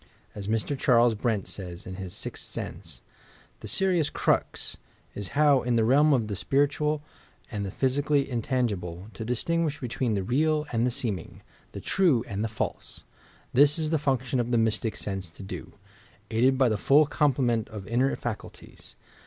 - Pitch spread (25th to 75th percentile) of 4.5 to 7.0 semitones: Yes, average, 5.0 semitones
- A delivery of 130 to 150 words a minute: No, average, 175 wpm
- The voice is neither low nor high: No, low, 120 Hz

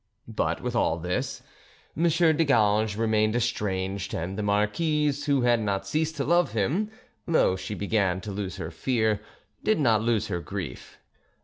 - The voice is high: No, low, 110 Hz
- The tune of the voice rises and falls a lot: Yes, wide, 6.4 semitones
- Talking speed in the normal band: Yes, average, 165 wpm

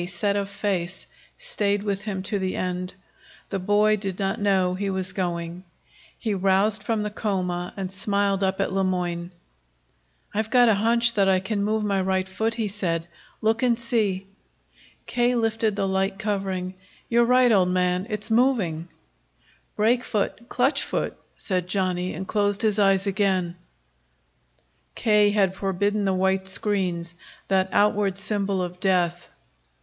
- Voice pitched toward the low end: No, high, 195 Hz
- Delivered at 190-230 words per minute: No, average, 155 wpm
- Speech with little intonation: Yes, narrow, 2.2 semitones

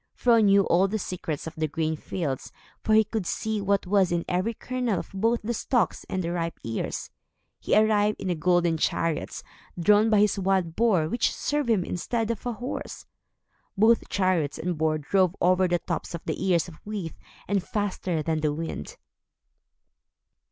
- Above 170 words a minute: Yes, average, 180 wpm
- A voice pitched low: No, medium, 185 Hz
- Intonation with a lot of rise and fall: No, average, 4.3 semitones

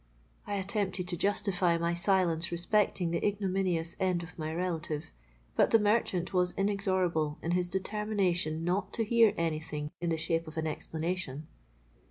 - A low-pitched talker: No, medium, 180 Hz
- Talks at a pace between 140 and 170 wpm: Yes, average, 160 wpm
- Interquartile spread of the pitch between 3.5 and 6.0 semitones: No, average, 3.0 semitones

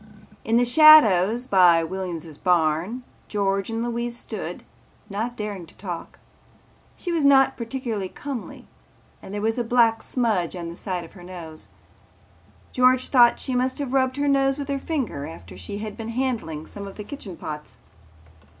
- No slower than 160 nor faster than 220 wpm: Yes, average, 170 wpm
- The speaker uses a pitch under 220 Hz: No, high, 225 Hz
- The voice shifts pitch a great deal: Yes, wide, 6.1 semitones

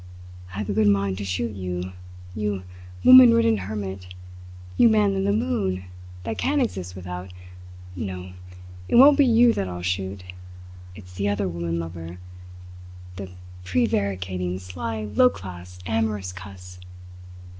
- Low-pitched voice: Yes, very low, 95 Hz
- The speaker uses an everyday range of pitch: Yes, average, 3.5 semitones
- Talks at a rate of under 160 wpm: Yes, average, 140 wpm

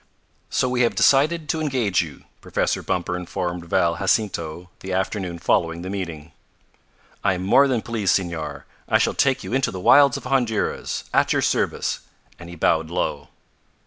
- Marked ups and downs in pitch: Yes, wide, 6.3 semitones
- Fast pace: No, average, 170 wpm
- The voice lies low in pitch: Yes, very low, 95 Hz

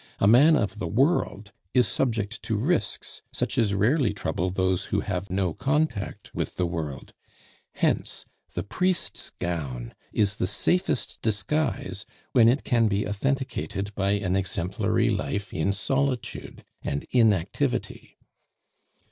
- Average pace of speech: No, slow, 130 wpm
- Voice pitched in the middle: No, low, 105 Hz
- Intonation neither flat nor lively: Yes, average, 5.0 semitones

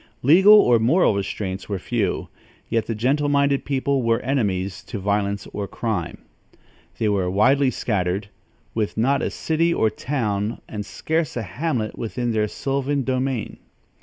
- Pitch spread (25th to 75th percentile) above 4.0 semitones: Yes, average, 5.2 semitones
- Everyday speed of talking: Yes, average, 150 wpm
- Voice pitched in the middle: No, low, 115 Hz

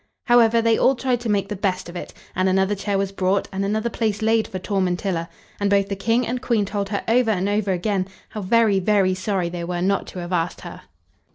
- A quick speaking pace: Yes, fast, 235 wpm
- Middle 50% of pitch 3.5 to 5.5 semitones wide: No, average, 2.8 semitones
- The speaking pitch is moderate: No, high, 200 Hz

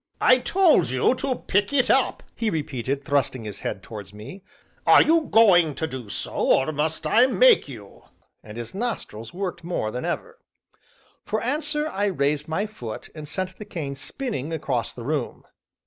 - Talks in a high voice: No, medium, 160 Hz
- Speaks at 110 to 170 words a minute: No, average, 180 wpm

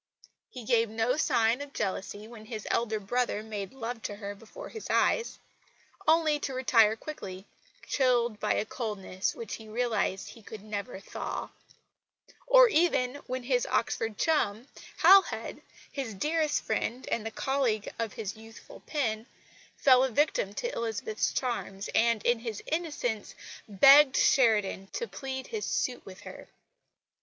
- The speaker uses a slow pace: No, average, 150 wpm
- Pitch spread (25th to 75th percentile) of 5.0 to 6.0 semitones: No, average, 4.1 semitones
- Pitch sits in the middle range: No, high, 230 Hz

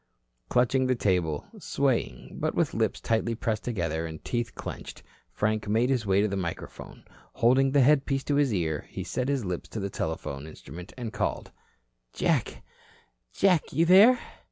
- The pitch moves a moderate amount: No, wide, 6.8 semitones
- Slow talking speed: No, average, 165 wpm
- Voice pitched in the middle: No, low, 110 Hz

